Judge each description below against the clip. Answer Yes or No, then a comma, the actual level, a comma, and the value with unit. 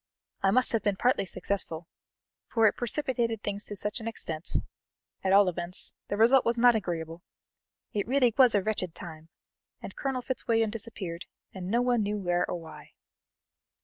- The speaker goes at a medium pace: Yes, average, 170 wpm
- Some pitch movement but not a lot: Yes, average, 4.6 semitones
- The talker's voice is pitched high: Yes, high, 210 Hz